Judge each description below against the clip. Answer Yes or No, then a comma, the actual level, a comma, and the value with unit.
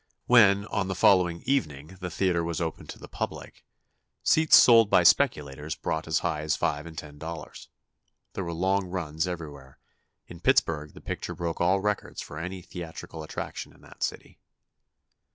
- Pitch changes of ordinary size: Yes, average, 3.4 semitones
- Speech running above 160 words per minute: Yes, average, 170 wpm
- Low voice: Yes, very low, 85 Hz